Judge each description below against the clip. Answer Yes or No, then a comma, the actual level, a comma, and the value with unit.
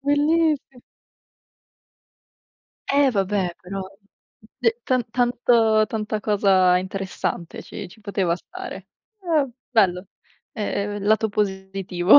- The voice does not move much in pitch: No, average, 4.8 semitones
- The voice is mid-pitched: No, high, 205 Hz